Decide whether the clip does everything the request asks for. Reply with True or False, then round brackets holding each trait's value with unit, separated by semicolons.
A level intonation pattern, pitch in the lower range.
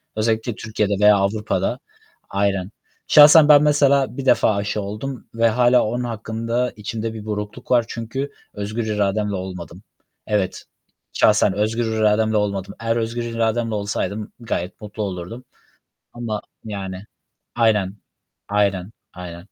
True (2.3 semitones; 110 Hz)